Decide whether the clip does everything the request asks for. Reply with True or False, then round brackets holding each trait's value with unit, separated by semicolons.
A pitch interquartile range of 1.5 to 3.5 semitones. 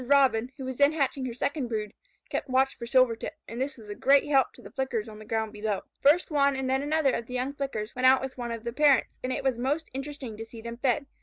True (3.1 semitones)